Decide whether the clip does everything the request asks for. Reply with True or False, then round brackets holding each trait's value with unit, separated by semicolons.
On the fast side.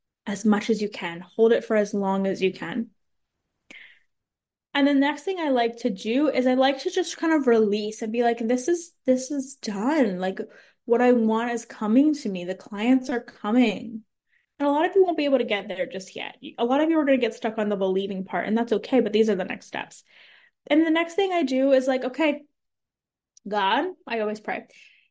True (230 wpm)